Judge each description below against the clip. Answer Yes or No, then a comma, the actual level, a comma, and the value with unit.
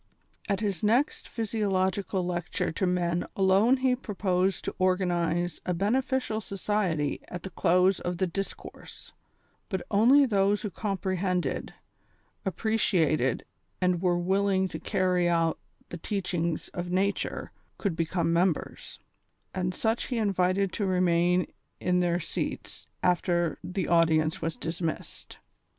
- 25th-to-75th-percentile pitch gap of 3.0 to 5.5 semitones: No, narrow, 2.5 semitones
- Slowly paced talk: Yes, slow, 130 wpm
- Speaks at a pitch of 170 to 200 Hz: Yes, medium, 185 Hz